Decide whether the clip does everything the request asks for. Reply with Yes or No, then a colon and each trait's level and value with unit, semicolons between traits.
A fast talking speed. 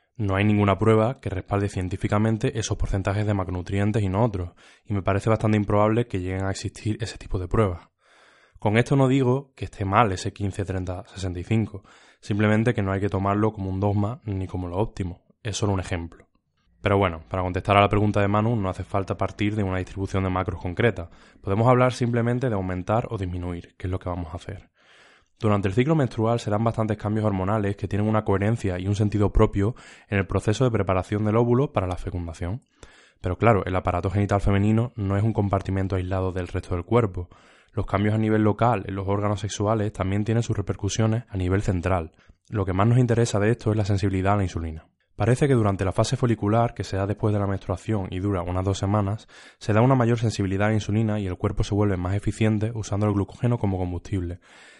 Yes: fast, 215 wpm